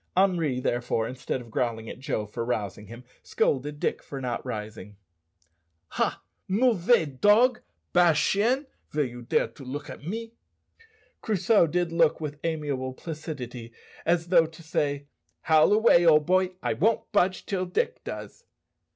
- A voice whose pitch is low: No, medium, 155 Hz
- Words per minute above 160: No, average, 150 wpm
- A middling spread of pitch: No, wide, 6.4 semitones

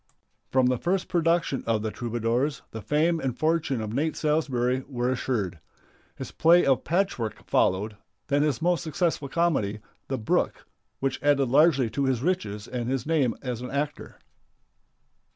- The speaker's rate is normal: Yes, average, 155 wpm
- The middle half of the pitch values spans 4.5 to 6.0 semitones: Yes, average, 4.8 semitones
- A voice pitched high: No, low, 135 Hz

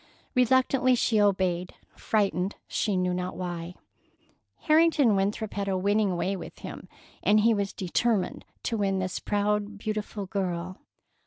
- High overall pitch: Yes, high, 200 Hz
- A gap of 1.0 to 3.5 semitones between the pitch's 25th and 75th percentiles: Yes, average, 2.7 semitones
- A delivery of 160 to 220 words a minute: No, average, 140 wpm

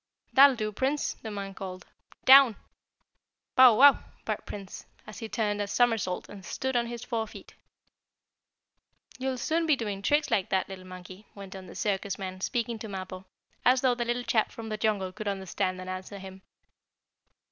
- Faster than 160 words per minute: Yes, average, 180 wpm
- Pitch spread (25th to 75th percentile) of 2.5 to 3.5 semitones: No, average, 4.1 semitones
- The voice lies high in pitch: Yes, high, 210 Hz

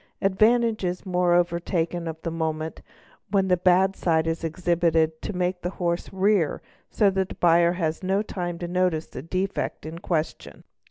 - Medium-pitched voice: Yes, medium, 175 Hz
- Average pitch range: No, narrow, 2.3 semitones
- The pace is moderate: Yes, average, 170 wpm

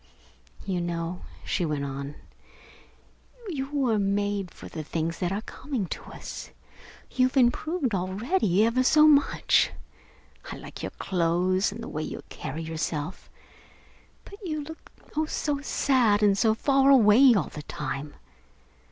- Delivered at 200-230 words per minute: No, average, 145 wpm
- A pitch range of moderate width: No, wide, 7.9 semitones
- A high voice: Yes, high, 205 Hz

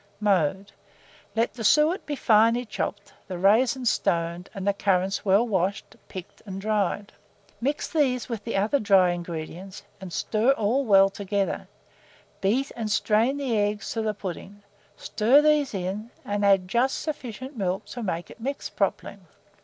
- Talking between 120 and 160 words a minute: Yes, average, 155 wpm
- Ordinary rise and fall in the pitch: Yes, average, 3.9 semitones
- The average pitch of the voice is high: Yes, high, 210 Hz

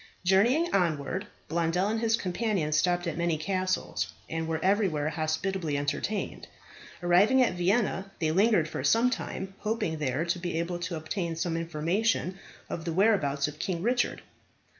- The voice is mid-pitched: Yes, medium, 175 Hz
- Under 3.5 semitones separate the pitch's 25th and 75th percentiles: No, average, 3.8 semitones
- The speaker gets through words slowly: No, average, 155 wpm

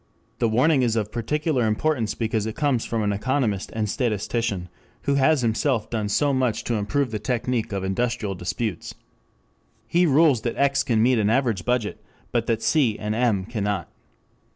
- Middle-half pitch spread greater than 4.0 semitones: No, average, 3.6 semitones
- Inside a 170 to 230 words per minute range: Yes, average, 175 wpm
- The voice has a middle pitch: No, low, 115 Hz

